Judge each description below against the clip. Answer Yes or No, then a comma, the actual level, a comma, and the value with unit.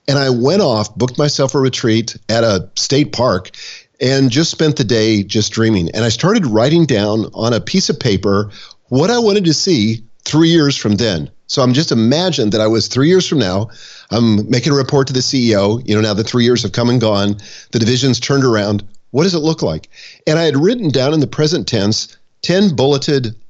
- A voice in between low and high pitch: No, low, 120 Hz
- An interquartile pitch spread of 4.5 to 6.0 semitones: Yes, average, 4.8 semitones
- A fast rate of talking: Yes, fast, 220 wpm